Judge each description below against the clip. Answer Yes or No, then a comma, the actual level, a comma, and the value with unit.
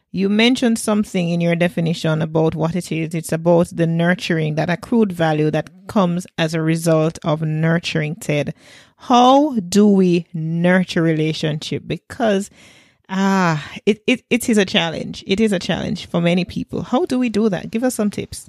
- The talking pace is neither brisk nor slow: Yes, average, 175 wpm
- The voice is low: No, medium, 175 Hz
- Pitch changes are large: No, average, 4.3 semitones